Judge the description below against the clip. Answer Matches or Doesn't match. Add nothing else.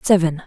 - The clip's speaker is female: Matches